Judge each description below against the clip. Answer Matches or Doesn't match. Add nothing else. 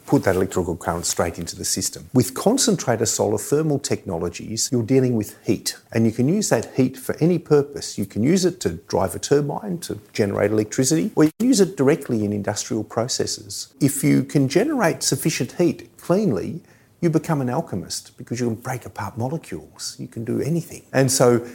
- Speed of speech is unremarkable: Matches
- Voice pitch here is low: Matches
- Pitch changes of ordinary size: Doesn't match